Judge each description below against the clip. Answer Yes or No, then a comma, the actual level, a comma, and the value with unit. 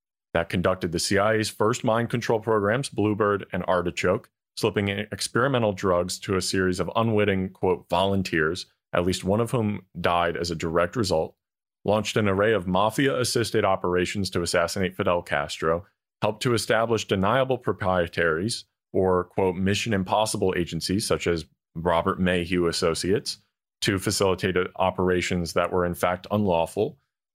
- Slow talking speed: No, average, 145 wpm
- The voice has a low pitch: Yes, very low, 95 Hz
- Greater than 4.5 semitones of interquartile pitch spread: No, average, 3.0 semitones